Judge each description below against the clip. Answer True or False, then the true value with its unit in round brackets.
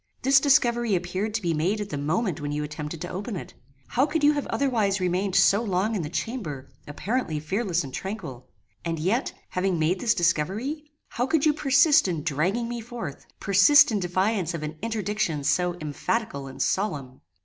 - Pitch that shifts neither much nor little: False (6.5 semitones)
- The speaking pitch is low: False (190 Hz)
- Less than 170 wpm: False (185 wpm)